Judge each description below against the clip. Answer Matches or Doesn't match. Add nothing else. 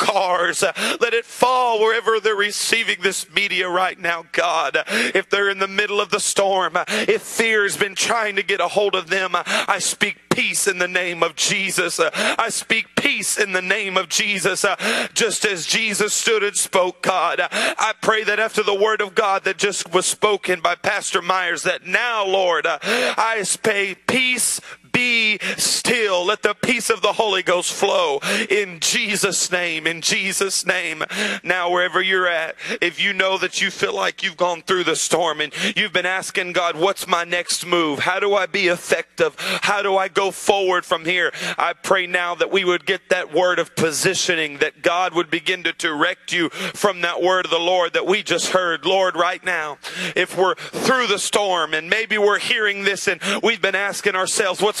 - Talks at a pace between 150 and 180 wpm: Doesn't match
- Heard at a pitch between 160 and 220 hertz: Matches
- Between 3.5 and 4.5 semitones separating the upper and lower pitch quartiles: Doesn't match